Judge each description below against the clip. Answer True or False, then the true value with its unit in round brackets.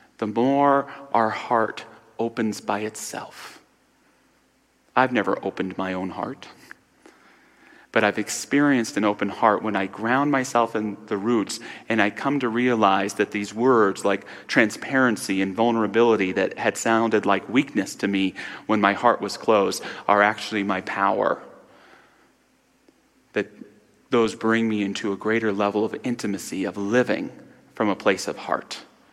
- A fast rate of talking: False (145 wpm)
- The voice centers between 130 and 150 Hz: False (110 Hz)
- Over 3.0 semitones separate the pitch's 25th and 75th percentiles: False (2.6 semitones)